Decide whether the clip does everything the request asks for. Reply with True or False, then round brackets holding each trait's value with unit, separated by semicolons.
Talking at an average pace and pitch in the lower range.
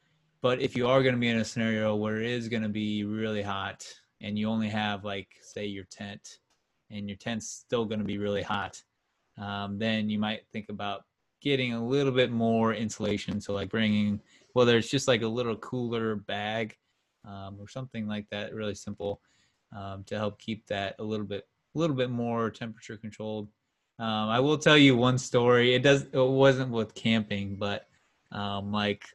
True (195 wpm; 110 Hz)